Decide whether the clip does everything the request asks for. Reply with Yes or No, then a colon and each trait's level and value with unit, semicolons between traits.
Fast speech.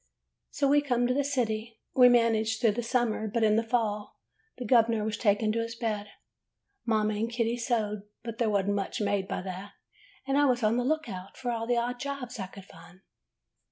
Yes: fast, 215 wpm